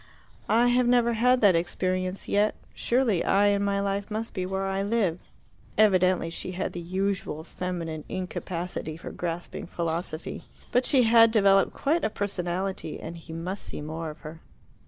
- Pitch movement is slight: No, average, 3.7 semitones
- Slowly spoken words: No, average, 165 wpm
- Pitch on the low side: No, high, 190 Hz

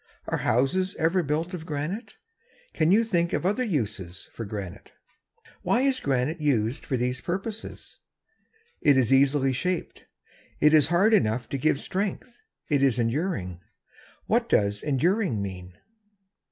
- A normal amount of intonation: No, wide, 7.1 semitones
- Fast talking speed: No, average, 140 wpm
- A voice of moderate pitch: Yes, medium, 145 Hz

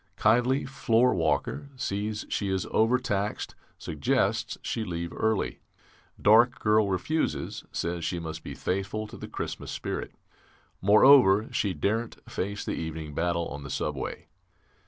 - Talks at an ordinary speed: No, slow, 130 wpm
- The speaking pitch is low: Yes, low, 100 Hz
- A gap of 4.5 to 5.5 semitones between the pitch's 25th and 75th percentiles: Yes, average, 4.9 semitones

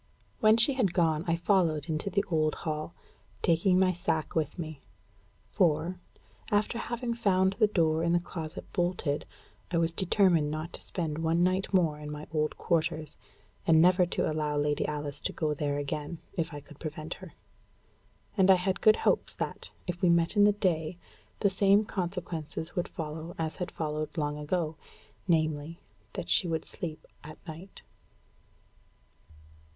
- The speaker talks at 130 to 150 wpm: No, average, 165 wpm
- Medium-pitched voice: Yes, medium, 165 Hz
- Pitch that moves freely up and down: No, average, 3.1 semitones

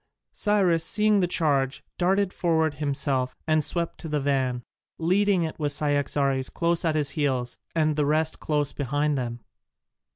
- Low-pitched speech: No, medium, 150 Hz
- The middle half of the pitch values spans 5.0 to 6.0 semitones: No, average, 3.3 semitones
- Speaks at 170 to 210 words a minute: No, average, 155 wpm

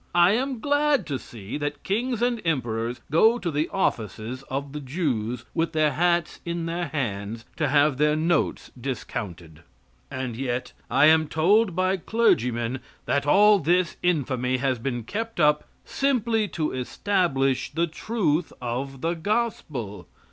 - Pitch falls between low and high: Yes, medium, 150 Hz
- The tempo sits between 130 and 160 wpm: Yes, average, 150 wpm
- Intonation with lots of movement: Yes, wide, 6.3 semitones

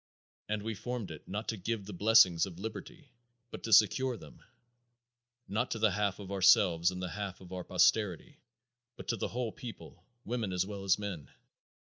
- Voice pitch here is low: Yes, low, 100 Hz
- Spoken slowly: No, average, 185 wpm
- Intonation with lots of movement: No, average, 3.3 semitones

